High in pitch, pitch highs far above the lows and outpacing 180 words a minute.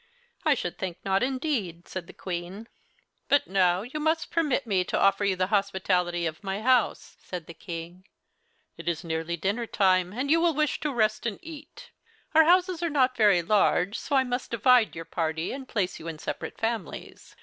Yes: high, 200 Hz; wide, 6.6 semitones; average, 195 wpm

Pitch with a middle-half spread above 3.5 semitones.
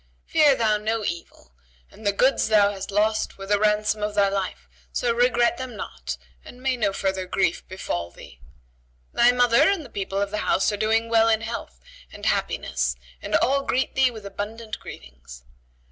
No: average, 3.2 semitones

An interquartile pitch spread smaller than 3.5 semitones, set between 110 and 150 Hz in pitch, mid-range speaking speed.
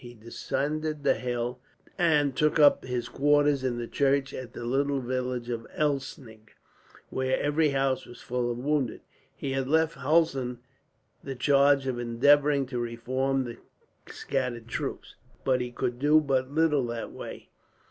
Yes: average, 2.9 semitones; low, 135 Hz; average, 155 wpm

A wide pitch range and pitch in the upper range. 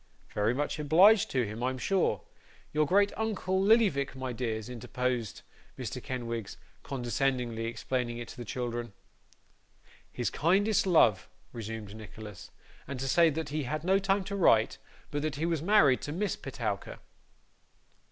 No: wide, 6.7 semitones; low, 135 Hz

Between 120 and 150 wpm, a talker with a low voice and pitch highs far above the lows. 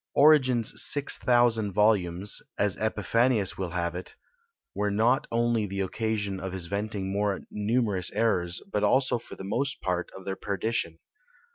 No: average, 145 wpm; low, 105 Hz; average, 3.4 semitones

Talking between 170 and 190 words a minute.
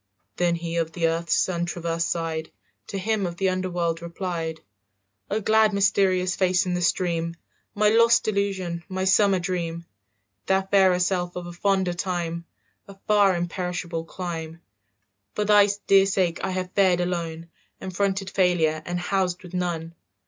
No: average, 160 wpm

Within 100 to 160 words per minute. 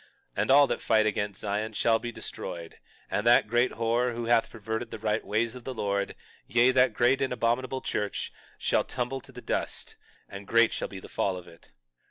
No: fast, 205 wpm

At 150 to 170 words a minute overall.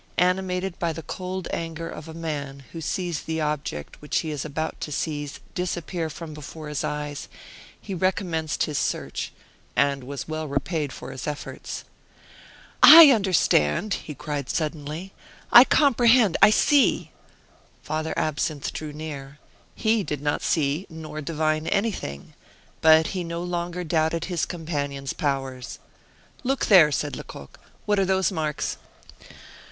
No: average, 140 wpm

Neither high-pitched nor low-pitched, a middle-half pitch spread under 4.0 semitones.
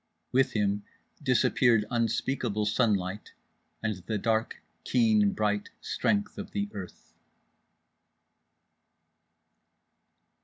No: low, 110 Hz; average, 3.2 semitones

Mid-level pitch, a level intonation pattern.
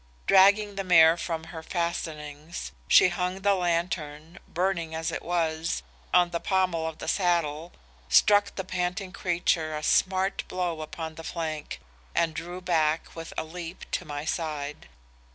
Yes: medium, 170 Hz; narrow, 2.3 semitones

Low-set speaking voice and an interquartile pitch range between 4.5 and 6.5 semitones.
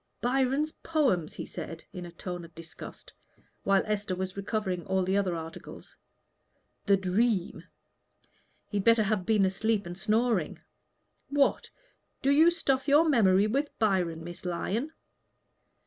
No: high, 200 Hz; average, 5.2 semitones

